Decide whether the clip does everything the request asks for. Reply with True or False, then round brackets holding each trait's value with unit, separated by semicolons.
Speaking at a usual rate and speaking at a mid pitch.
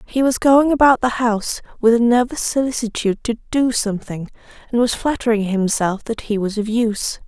False (180 wpm; 230 Hz)